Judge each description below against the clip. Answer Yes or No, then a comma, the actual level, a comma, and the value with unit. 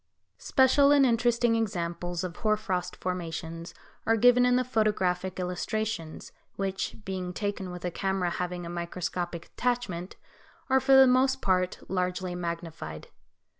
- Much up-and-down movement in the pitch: No, average, 4.4 semitones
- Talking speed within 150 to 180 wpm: No, slow, 135 wpm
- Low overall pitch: No, medium, 185 Hz